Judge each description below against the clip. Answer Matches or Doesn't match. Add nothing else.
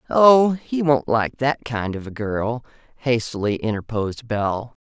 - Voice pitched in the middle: Doesn't match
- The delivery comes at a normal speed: Matches